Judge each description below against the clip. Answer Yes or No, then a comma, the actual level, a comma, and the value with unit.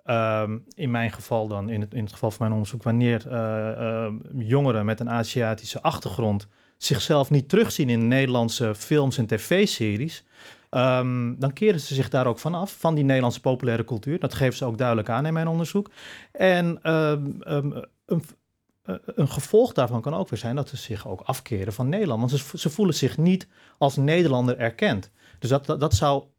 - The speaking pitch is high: No, low, 130 Hz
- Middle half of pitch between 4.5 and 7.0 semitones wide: Yes, average, 4.8 semitones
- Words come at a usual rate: Yes, average, 190 wpm